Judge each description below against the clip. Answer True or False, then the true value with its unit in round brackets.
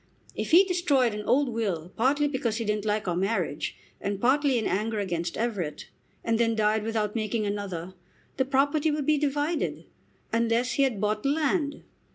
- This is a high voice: True (230 Hz)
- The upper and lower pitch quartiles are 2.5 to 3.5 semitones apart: False (5.1 semitones)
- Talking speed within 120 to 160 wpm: False (175 wpm)